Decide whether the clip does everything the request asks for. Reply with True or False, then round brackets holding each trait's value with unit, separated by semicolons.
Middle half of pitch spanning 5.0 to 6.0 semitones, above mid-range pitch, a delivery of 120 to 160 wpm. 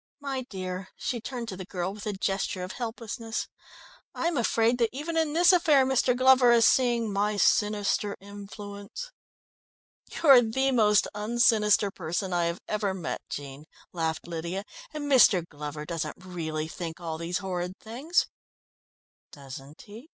True (5.5 semitones; 205 Hz; 155 wpm)